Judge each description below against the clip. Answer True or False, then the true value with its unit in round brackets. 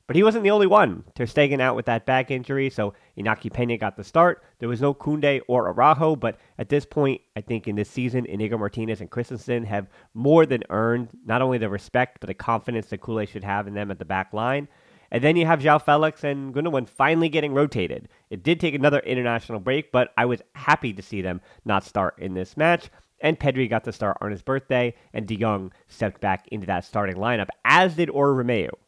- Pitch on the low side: True (120 Hz)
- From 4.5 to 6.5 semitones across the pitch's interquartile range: True (4.9 semitones)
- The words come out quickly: True (225 wpm)